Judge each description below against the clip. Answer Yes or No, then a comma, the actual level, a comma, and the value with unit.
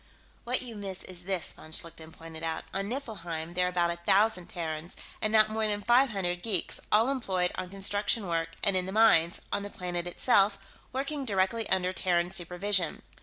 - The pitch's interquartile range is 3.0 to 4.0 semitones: Yes, average, 3.7 semitones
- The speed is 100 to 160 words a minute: No, average, 190 wpm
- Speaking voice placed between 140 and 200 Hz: Yes, high, 190 Hz